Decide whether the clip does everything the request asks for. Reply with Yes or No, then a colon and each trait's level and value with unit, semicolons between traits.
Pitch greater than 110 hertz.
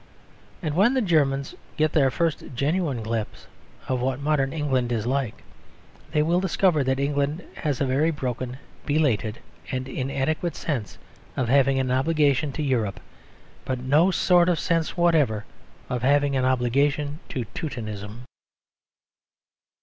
Yes: medium, 140 Hz